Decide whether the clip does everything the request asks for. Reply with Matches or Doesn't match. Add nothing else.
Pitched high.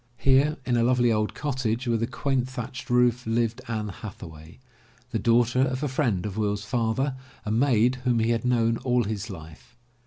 Doesn't match